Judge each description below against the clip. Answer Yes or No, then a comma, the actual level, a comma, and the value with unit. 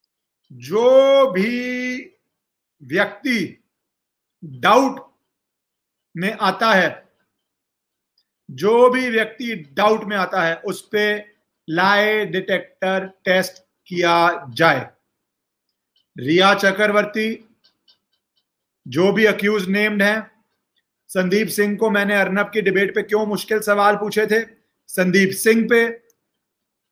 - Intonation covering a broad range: No, narrow, 2.5 semitones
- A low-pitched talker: No, high, 205 Hz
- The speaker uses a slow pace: Yes, slow, 100 wpm